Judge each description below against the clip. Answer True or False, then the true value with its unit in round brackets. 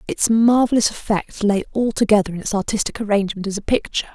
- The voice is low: False (210 Hz)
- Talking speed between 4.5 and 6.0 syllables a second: False (6.5 syllables/s)